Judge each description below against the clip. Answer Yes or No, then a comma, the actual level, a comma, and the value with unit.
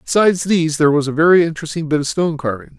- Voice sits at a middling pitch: Yes, medium, 160 Hz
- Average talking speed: No, fast, 235 wpm